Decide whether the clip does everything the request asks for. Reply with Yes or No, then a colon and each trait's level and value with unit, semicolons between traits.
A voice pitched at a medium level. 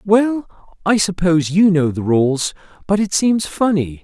Yes: medium, 180 Hz